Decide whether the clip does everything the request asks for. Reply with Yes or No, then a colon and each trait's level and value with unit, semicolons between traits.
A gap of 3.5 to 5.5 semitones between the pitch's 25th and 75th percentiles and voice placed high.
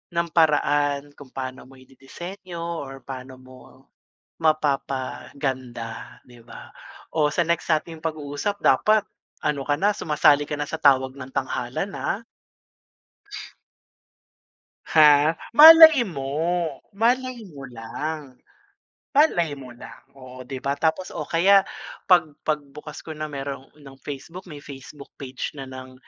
No: average, 3.8 semitones; medium, 145 Hz